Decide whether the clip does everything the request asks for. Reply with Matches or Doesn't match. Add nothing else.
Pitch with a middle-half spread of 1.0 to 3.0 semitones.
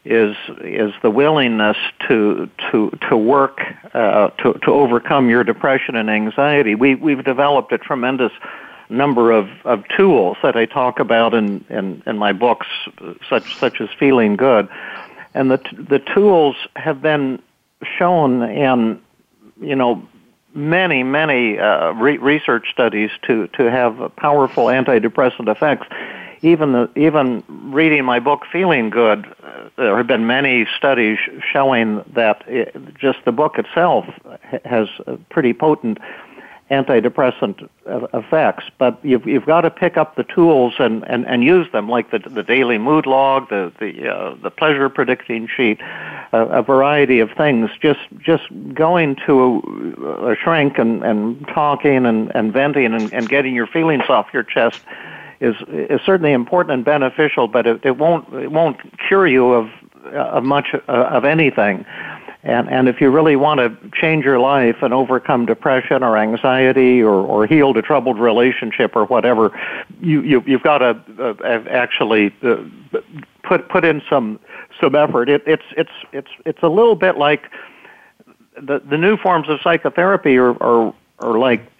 Doesn't match